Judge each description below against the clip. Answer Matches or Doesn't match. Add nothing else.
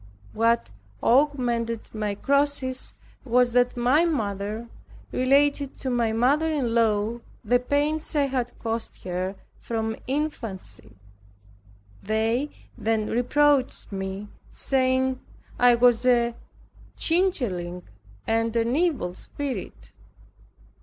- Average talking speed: Doesn't match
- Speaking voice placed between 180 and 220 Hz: Doesn't match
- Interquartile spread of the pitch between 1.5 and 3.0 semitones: Doesn't match